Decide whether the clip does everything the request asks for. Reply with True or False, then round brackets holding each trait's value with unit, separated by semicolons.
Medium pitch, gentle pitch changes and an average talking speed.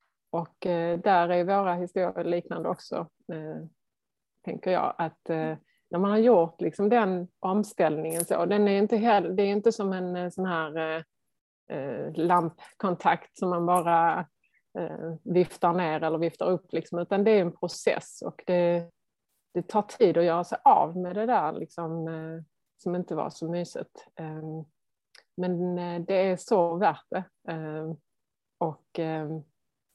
True (175 Hz; 2.3 semitones; 160 wpm)